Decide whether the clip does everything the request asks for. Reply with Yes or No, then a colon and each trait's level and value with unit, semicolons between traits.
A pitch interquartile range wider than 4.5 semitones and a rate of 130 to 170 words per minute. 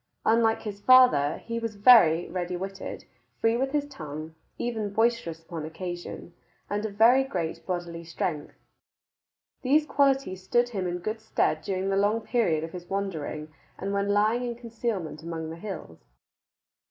Yes: wide, 5.5 semitones; average, 155 wpm